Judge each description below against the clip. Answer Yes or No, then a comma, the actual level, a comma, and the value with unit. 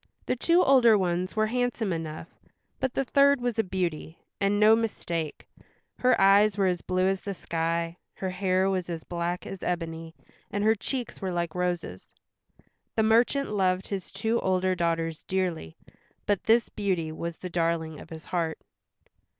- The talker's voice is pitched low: No, medium, 185 Hz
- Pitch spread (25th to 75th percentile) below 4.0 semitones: No, average, 4.3 semitones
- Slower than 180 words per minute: Yes, average, 165 wpm